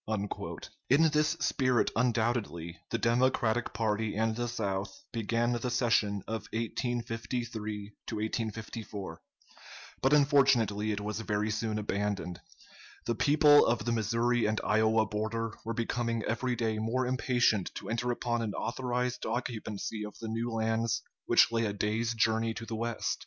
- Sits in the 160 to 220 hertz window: No, low, 115 Hz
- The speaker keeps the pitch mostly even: Yes, narrow, 2.1 semitones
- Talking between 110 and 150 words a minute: Yes, average, 140 wpm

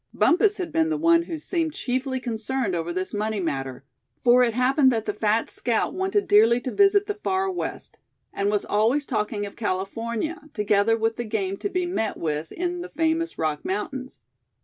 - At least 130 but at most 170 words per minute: No, average, 190 wpm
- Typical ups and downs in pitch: No, wide, 7.9 semitones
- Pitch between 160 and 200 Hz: No, high, 240 Hz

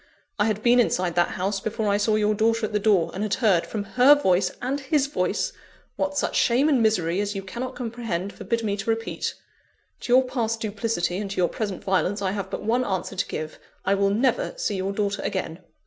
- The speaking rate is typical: No, fast, 225 wpm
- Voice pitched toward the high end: Yes, high, 210 Hz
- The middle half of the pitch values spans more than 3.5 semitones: No, average, 3.2 semitones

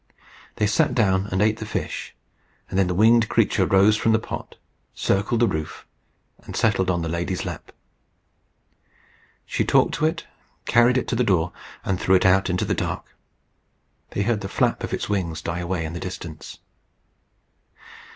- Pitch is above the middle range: No, very low, 95 Hz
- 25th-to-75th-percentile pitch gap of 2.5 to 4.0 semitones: Yes, average, 3.6 semitones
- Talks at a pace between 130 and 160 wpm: No, average, 175 wpm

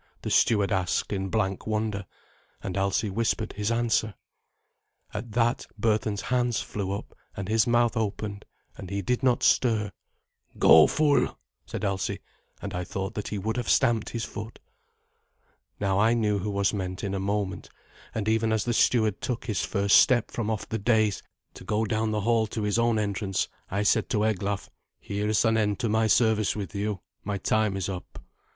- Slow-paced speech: No, average, 185 wpm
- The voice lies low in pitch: Yes, low, 105 Hz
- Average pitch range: No, narrow, 2.0 semitones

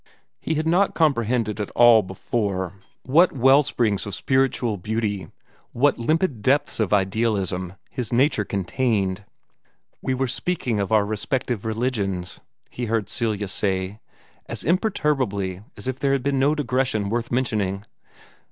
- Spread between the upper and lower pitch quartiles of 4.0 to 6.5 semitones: Yes, average, 4.6 semitones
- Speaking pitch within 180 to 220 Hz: No, low, 115 Hz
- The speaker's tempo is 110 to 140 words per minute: Yes, slow, 135 wpm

